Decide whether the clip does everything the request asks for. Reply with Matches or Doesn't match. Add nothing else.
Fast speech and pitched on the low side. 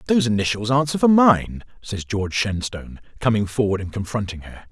Doesn't match